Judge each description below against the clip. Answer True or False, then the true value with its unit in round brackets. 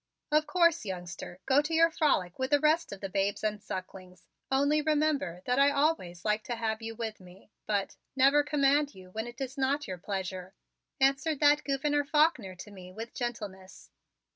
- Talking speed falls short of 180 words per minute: False (185 wpm)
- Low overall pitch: False (240 Hz)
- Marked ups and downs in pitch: True (7.3 semitones)